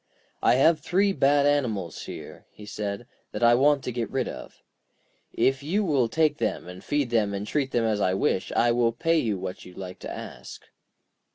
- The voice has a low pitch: Yes, low, 120 Hz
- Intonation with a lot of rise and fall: Yes, wide, 5.9 semitones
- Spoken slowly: No, average, 200 wpm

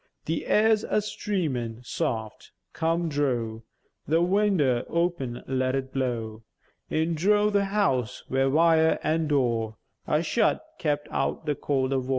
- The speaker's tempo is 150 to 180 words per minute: No, average, 140 wpm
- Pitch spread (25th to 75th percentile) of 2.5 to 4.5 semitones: No, average, 5.1 semitones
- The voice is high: No, medium, 145 Hz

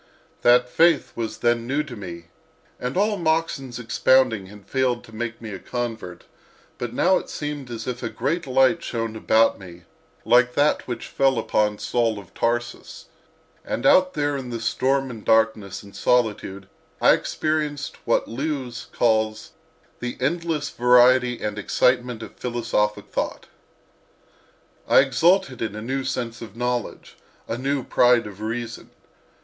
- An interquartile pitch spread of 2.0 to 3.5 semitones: Yes, average, 3.2 semitones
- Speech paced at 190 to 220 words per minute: No, average, 150 wpm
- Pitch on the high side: No, low, 120 Hz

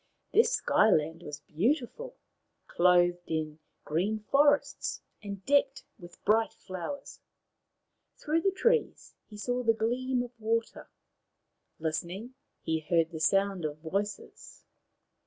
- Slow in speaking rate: Yes, slow, 120 wpm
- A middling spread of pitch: No, wide, 6.8 semitones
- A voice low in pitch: No, high, 205 Hz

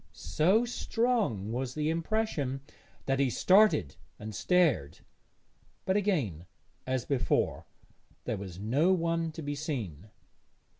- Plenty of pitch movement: Yes, wide, 8.7 semitones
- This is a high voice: No, medium, 145 Hz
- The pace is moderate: No, slow, 115 wpm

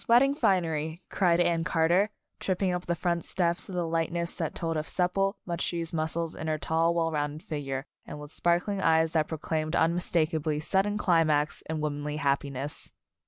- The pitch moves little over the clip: Yes, narrow, 2.2 semitones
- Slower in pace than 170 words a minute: No, average, 180 wpm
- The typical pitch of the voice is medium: Yes, medium, 165 Hz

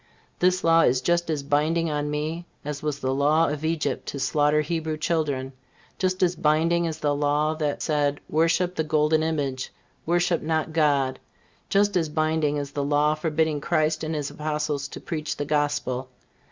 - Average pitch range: No, narrow, 1.8 semitones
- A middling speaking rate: Yes, average, 175 wpm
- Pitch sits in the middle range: Yes, medium, 155 Hz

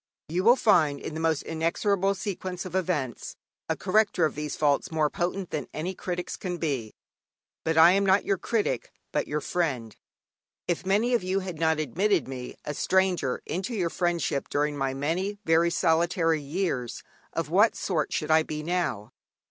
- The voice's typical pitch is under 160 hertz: No, medium, 170 Hz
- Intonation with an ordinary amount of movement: Yes, average, 3.8 semitones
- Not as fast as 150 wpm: No, average, 170 wpm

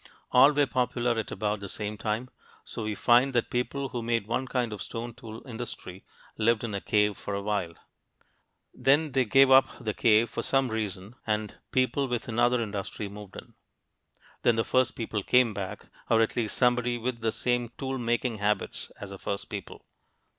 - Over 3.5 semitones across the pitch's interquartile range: No, average, 2.9 semitones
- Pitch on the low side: Yes, low, 115 Hz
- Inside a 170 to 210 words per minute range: Yes, average, 190 wpm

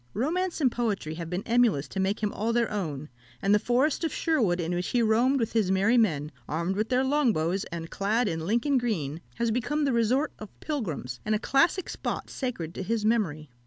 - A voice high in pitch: Yes, high, 215 Hz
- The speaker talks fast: Yes, fast, 215 wpm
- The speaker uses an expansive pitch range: Yes, wide, 6.0 semitones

